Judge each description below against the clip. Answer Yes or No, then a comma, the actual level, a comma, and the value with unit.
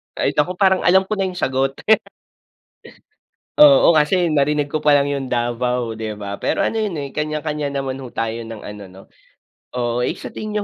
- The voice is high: No, medium, 140 Hz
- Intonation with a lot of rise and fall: Yes, wide, 6.5 semitones